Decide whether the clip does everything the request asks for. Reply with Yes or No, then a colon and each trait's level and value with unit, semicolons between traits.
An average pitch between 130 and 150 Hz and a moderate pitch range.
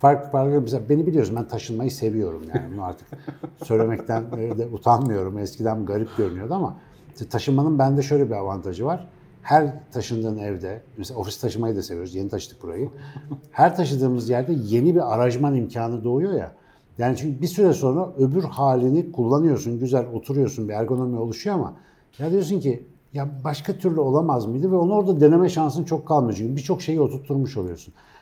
Yes: low, 135 Hz; average, 4.8 semitones